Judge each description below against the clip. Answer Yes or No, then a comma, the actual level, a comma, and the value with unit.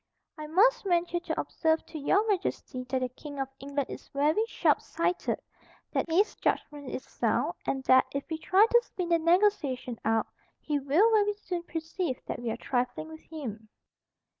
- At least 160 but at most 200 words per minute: Yes, average, 175 wpm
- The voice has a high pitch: Yes, very high, 315 Hz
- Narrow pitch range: No, average, 5.2 semitones